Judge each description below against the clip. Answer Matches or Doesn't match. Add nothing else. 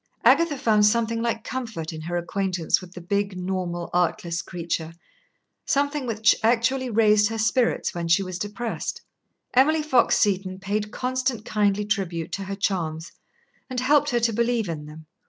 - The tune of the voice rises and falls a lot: Doesn't match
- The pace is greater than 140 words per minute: Matches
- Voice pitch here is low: Doesn't match